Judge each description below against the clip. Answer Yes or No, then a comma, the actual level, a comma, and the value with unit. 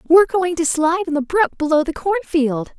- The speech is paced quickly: Yes, fast, 215 wpm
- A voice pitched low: No, very high, 325 Hz